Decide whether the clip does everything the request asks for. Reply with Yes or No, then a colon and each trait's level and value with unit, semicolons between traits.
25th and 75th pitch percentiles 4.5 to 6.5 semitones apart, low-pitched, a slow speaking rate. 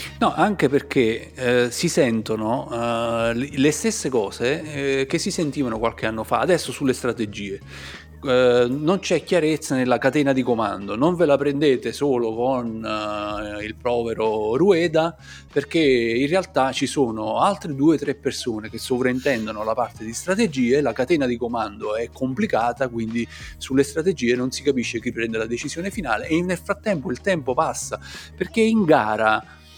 No: average, 5.1 semitones; low, 125 Hz; average, 160 wpm